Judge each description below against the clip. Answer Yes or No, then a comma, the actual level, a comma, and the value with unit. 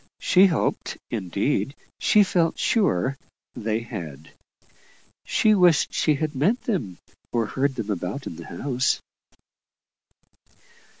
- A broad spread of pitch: Yes, wide, 8.4 semitones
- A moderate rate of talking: No, slow, 115 wpm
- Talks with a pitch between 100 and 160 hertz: Yes, low, 135 Hz